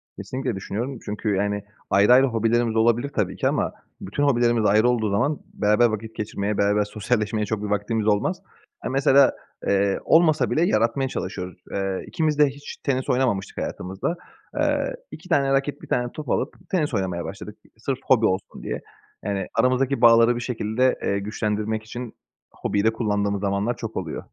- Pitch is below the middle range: Yes, low, 110 Hz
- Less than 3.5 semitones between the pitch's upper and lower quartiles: No, average, 3.9 semitones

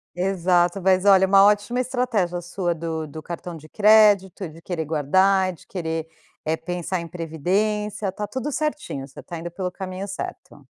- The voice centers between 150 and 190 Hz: Yes, medium, 185 Hz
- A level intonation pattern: No, average, 3.3 semitones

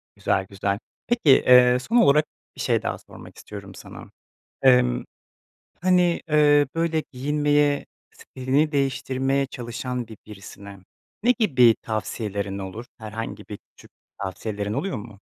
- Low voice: Yes, low, 125 Hz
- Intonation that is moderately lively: No, wide, 6.2 semitones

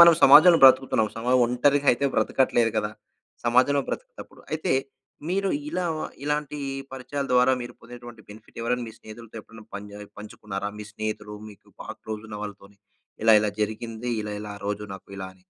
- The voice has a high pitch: No, low, 115 Hz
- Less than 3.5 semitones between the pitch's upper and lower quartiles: No, average, 4.2 semitones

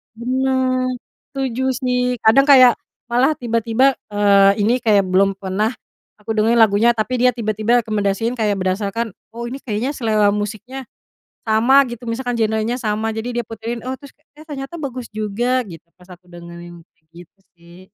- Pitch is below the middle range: No, high, 225 Hz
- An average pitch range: Yes, average, 3.6 semitones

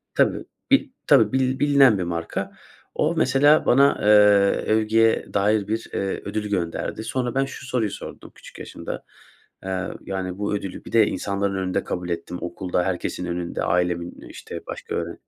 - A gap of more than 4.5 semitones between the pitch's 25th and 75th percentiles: Yes, average, 5.3 semitones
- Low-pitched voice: Yes, low, 100 Hz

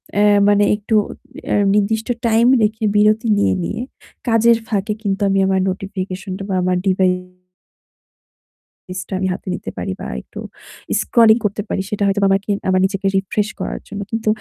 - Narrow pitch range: Yes, narrow, 2.2 semitones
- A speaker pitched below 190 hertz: No, high, 205 Hz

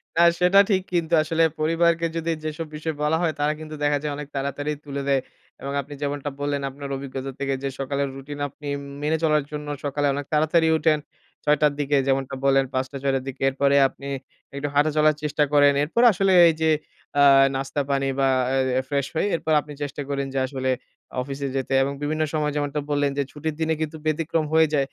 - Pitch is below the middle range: No, medium, 145 Hz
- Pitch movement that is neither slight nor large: No, narrow, 2.0 semitones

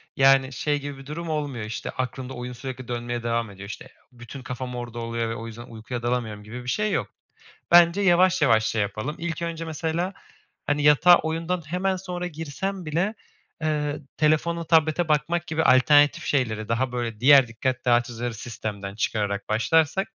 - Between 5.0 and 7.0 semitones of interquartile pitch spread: Yes, wide, 5.6 semitones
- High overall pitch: No, low, 135 Hz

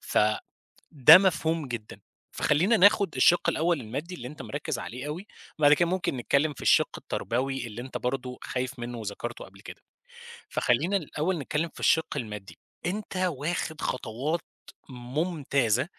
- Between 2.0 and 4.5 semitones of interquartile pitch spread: No, wide, 5.4 semitones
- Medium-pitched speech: Yes, medium, 145 Hz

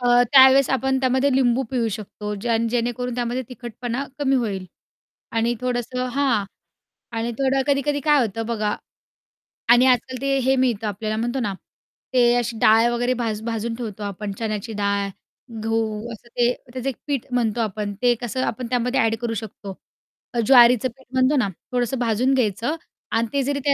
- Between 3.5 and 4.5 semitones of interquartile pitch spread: No, average, 2.7 semitones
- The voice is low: No, high, 240 Hz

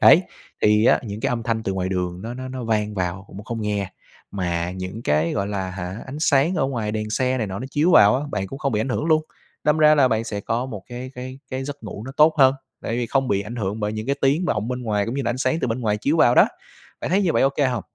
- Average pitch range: Yes, average, 4.5 semitones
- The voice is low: Yes, low, 115 Hz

